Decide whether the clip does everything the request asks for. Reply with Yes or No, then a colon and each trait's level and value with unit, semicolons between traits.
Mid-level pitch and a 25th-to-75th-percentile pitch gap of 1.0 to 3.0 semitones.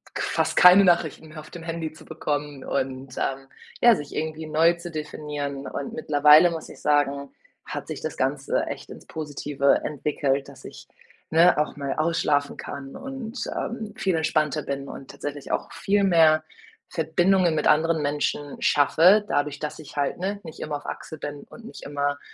Yes: medium, 150 Hz; average, 2.7 semitones